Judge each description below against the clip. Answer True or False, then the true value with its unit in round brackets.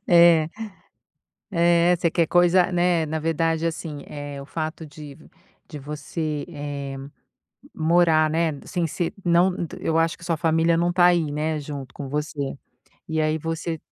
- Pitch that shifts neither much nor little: False (2.2 semitones)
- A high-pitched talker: False (160 Hz)